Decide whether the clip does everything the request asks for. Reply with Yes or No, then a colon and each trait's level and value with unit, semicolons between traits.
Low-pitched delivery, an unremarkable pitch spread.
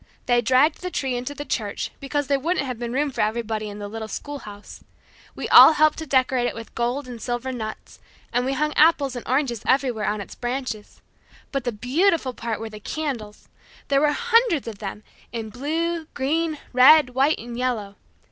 No: very high, 255 Hz; average, 4.2 semitones